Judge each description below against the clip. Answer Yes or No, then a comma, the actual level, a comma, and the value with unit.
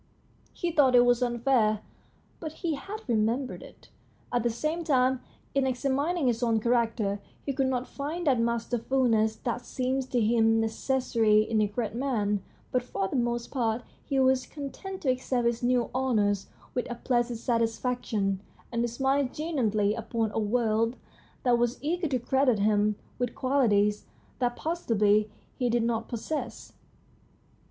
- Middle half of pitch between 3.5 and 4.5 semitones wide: No, average, 2.9 semitones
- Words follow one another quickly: No, average, 160 wpm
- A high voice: Yes, high, 240 Hz